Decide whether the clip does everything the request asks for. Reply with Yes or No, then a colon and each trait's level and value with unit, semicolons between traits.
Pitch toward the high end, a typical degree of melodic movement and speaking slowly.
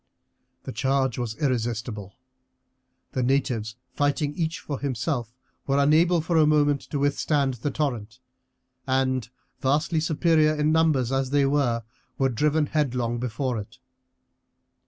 No: low, 135 Hz; average, 3.7 semitones; slow, 130 wpm